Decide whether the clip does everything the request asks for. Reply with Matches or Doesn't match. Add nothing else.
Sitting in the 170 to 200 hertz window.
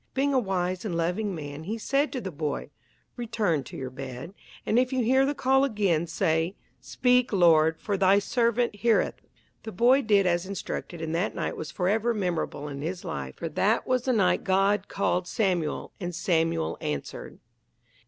Matches